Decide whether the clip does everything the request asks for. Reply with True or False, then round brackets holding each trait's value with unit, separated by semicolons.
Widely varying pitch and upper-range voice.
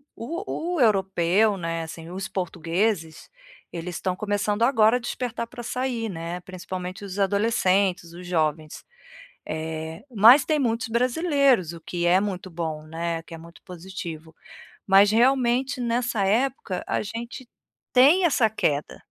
True (5.8 semitones; 195 Hz)